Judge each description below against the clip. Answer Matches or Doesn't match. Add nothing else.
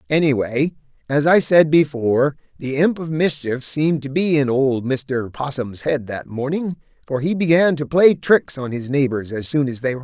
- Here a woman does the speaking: Doesn't match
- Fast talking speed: Matches